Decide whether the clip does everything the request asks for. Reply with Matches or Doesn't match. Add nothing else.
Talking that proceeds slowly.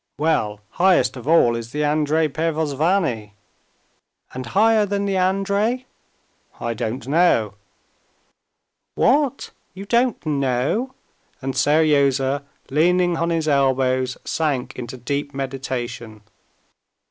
Matches